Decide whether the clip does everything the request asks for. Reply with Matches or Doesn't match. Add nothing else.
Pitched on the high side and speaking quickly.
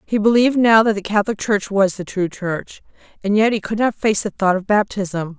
Matches